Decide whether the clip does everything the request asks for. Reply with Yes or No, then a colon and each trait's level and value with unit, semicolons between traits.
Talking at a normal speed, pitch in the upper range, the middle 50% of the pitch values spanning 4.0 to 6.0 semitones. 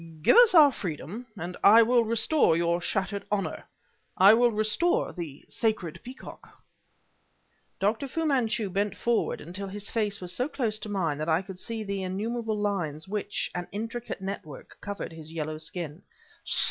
Yes: average, 160 wpm; high, 205 Hz; average, 4.5 semitones